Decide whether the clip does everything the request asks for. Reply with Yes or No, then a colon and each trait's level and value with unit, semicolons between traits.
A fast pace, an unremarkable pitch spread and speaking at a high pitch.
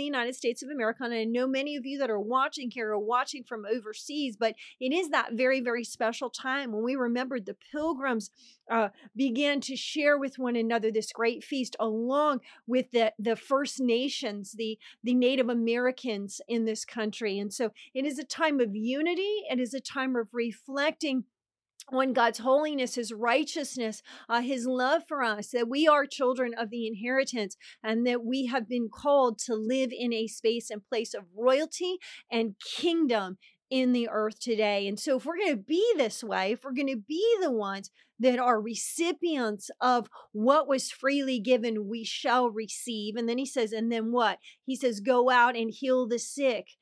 No: average, 190 wpm; average, 3.1 semitones; high, 245 Hz